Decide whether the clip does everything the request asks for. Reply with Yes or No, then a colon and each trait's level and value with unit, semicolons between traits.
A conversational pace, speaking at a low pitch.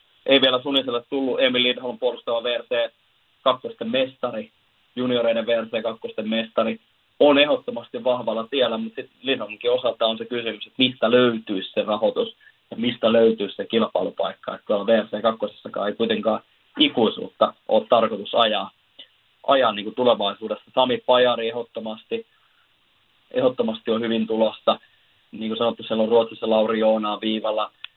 Yes: average, 135 wpm; low, 115 Hz